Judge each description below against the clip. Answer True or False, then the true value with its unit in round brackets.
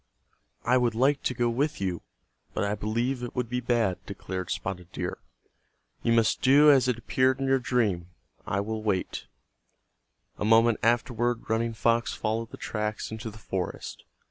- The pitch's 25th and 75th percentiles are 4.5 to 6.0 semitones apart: False (2.6 semitones)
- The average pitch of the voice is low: True (115 Hz)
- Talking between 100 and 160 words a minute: False (170 wpm)